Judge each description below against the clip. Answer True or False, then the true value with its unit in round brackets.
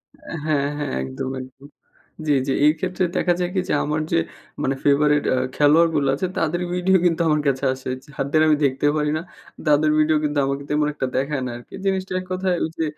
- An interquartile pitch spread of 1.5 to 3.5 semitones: True (2.9 semitones)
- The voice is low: False (150 Hz)